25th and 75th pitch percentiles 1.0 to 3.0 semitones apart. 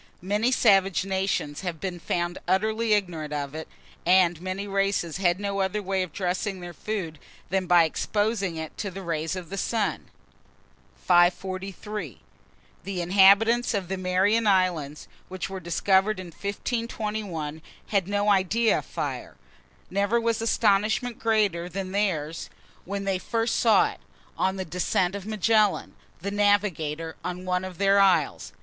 Yes: average, 2.7 semitones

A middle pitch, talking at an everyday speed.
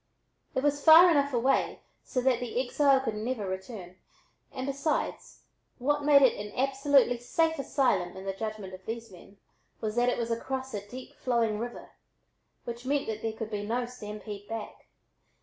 No: high, 240 Hz; average, 175 wpm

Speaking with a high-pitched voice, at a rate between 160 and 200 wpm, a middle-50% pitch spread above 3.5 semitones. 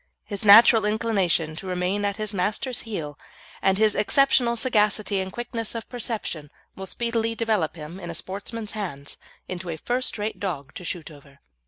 Yes: high, 205 Hz; average, 170 wpm; average, 4.2 semitones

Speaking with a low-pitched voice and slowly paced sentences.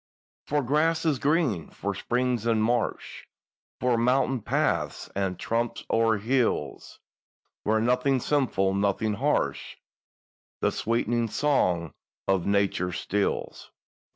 Yes: low, 115 Hz; slow, 100 wpm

